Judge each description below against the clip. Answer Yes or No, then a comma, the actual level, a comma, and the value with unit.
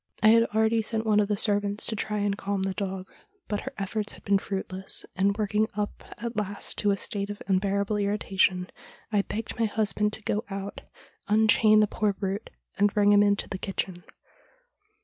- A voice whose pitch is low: No, high, 205 Hz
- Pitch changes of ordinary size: No, narrow, 1.4 semitones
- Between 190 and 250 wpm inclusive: Yes, average, 195 wpm